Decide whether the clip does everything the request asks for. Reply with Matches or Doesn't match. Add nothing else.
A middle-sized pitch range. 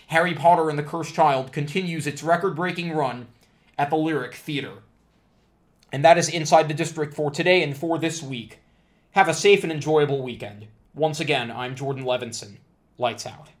Matches